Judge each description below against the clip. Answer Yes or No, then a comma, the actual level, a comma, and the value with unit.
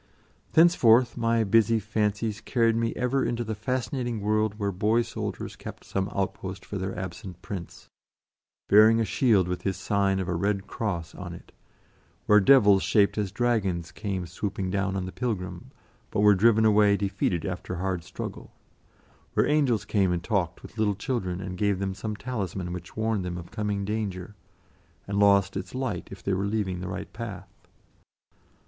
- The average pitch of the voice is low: Yes, low, 100 Hz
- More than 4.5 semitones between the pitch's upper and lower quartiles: No, average, 2.8 semitones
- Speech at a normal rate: Yes, average, 170 wpm